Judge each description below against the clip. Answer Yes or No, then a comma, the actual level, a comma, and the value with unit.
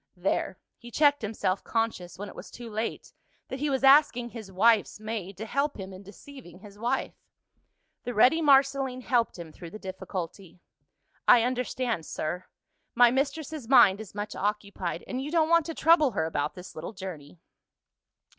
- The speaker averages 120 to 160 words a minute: No, average, 170 wpm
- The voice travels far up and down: Yes, wide, 5.9 semitones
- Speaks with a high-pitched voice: Yes, high, 225 Hz